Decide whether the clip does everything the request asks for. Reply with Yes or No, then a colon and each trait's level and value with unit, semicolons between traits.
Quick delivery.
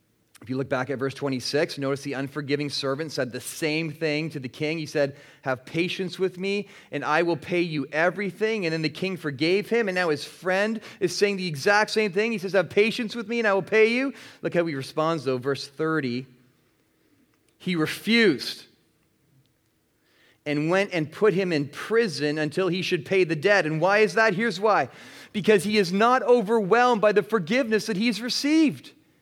No: average, 195 wpm